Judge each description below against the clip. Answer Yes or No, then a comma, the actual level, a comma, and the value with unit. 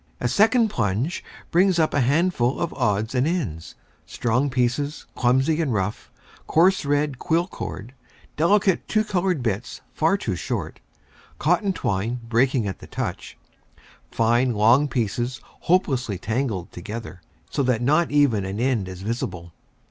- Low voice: Yes, low, 130 Hz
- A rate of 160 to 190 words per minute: No, average, 140 wpm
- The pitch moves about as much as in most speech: No, wide, 6.4 semitones